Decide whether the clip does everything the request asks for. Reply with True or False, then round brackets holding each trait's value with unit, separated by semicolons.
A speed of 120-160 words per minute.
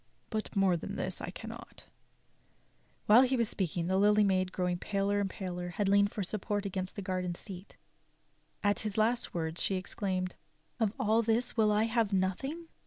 False (180 wpm)